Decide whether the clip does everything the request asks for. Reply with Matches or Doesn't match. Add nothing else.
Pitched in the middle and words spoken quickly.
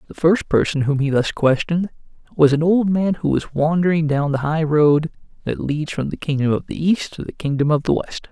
Matches